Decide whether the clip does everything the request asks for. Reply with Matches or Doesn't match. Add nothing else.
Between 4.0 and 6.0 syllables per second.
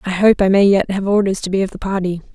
Doesn't match